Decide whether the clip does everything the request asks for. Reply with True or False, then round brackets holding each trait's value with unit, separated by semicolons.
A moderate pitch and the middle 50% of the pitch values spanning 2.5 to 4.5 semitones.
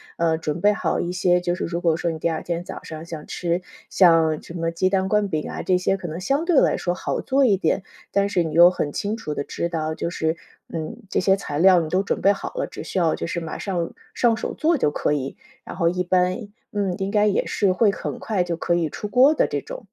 True (180 Hz; 3.3 semitones)